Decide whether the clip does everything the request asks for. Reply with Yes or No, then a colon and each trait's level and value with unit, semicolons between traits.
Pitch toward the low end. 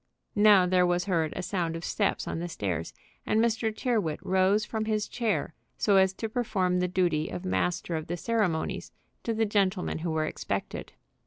No: medium, 185 Hz